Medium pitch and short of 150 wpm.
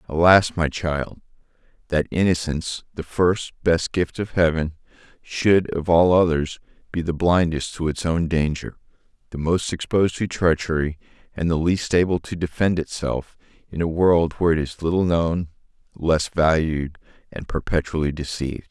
No: very low, 80 Hz; average, 140 wpm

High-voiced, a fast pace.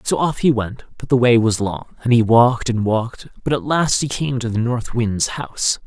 No: low, 120 Hz; fast, 245 wpm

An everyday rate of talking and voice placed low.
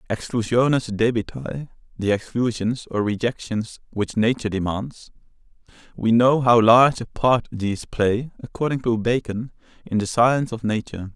No: slow, 125 wpm; low, 115 Hz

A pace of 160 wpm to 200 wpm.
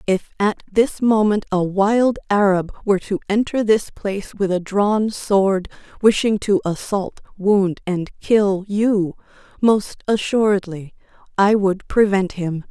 No: slow, 135 wpm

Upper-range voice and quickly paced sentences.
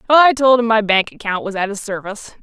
Yes: high, 220 Hz; fast, 250 wpm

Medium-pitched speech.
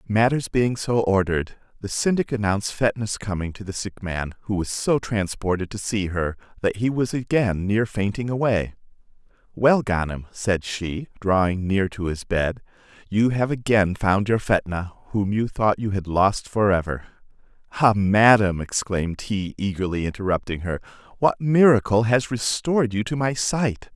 No: low, 105 Hz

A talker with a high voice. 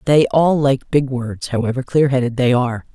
No: low, 130 Hz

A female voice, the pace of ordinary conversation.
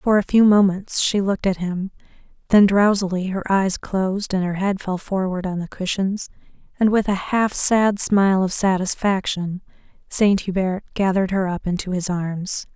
Yes: female; average, 175 wpm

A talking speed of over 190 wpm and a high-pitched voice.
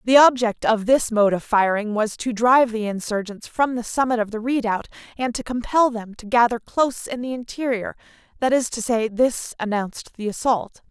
Yes: average, 200 wpm; high, 230 Hz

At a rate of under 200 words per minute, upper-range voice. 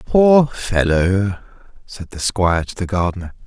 No: average, 140 wpm; low, 100 Hz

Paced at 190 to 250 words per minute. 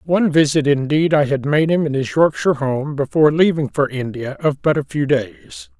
Yes: fast, 205 wpm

